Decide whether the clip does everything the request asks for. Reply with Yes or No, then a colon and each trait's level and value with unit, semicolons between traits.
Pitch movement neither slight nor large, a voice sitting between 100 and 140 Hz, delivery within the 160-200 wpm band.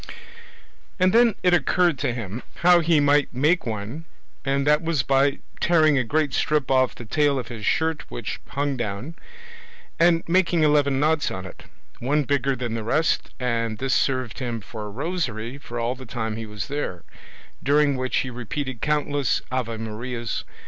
Yes: average, 4.4 semitones; low, 135 Hz; average, 170 wpm